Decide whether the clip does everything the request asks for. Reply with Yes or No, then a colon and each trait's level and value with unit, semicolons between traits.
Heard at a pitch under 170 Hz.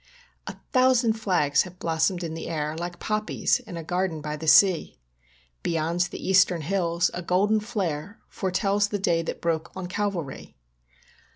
No: medium, 180 Hz